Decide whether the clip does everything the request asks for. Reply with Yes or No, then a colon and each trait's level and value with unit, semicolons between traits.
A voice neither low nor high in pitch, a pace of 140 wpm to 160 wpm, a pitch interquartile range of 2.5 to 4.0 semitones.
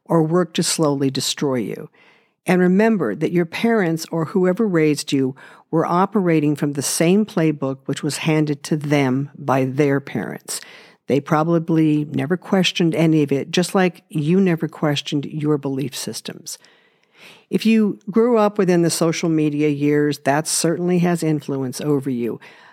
Yes: medium, 160 Hz; average, 155 wpm; average, 3.5 semitones